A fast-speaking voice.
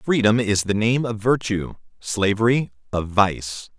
No: average, 145 wpm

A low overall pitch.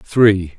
Yes: low, 100 Hz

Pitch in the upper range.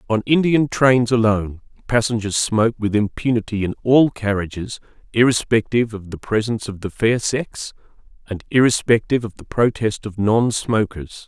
No: low, 110 Hz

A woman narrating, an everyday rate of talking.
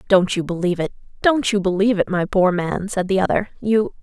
No: female; fast, 225 wpm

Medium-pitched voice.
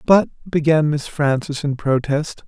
Yes: medium, 145 Hz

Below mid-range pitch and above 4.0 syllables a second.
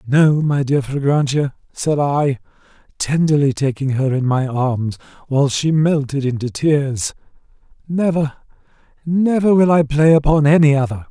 No: medium, 145 Hz; 4.5 syllables/s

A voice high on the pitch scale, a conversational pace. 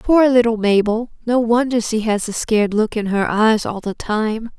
No: high, 225 Hz; fast, 210 wpm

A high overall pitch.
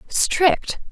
Yes: very high, 345 Hz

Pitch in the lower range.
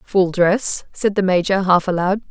No: high, 190 Hz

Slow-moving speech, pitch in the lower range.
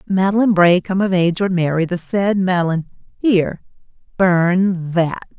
No: slow, 110 wpm; medium, 180 Hz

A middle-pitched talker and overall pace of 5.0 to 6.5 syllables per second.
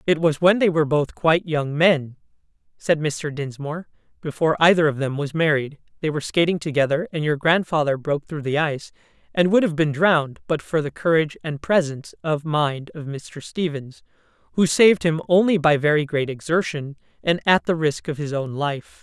Yes: medium, 155 Hz; 5.5 syllables/s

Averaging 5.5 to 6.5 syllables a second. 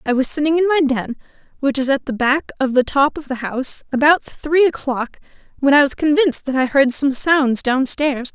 No: 5.2 syllables/s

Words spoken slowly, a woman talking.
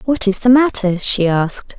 No: average, 200 wpm; female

